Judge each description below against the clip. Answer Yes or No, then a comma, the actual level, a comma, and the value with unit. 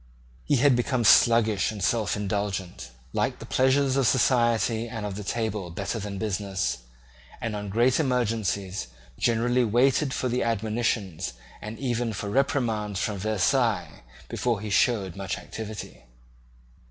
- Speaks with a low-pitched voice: Yes, low, 110 Hz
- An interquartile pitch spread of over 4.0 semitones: No, average, 3.2 semitones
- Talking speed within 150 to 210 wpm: No, slow, 135 wpm